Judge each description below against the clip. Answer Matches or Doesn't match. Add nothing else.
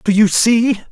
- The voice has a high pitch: Matches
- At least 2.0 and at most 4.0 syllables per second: Matches